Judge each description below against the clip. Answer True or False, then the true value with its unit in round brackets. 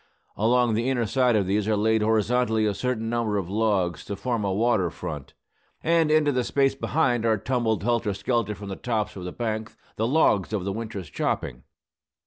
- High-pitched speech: False (110 Hz)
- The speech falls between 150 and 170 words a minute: False (195 wpm)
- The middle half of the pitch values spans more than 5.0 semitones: False (3.2 semitones)